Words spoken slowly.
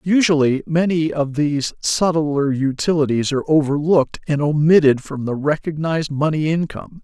Yes: slow, 130 wpm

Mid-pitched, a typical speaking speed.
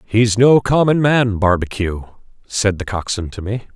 No: low, 110 Hz; average, 160 wpm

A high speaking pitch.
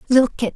Yes: high, 235 Hz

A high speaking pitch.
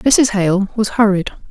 Yes: high, 205 Hz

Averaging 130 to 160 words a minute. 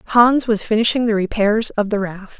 No: average, 200 wpm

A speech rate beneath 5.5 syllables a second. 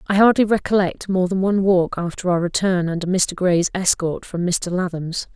Yes: 5.1 syllables/s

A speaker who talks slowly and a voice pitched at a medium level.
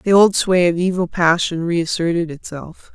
No: average, 165 wpm; medium, 175 Hz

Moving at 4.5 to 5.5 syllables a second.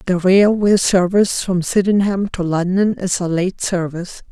Yes: 4.7 syllables/s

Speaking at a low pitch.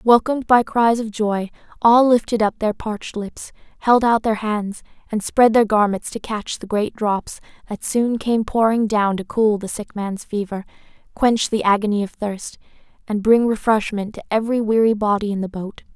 No: high, 215 Hz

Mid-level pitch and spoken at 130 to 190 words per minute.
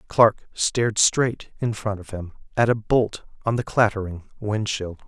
No: low, 105 Hz; average, 175 wpm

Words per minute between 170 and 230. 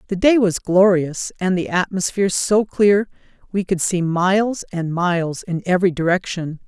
No: average, 160 wpm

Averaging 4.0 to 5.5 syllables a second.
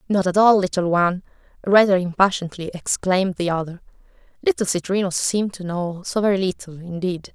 No: 5.8 syllables/s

